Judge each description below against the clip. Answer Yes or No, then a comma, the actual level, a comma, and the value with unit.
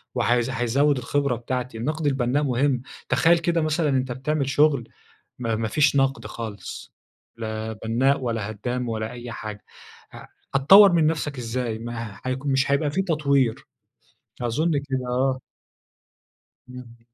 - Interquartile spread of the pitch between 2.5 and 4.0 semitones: Yes, average, 3.6 semitones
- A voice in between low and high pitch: No, low, 130 Hz